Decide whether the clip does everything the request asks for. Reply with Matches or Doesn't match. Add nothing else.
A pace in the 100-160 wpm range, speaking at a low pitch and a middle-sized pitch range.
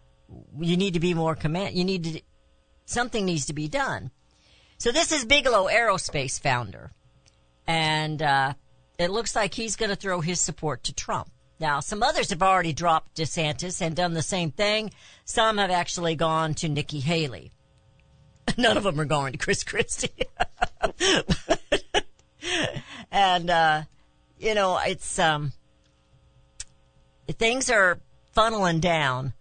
Doesn't match